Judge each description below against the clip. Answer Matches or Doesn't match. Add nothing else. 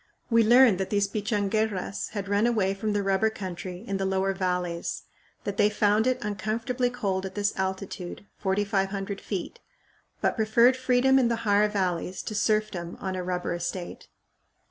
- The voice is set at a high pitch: Matches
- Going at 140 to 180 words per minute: Matches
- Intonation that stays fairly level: Matches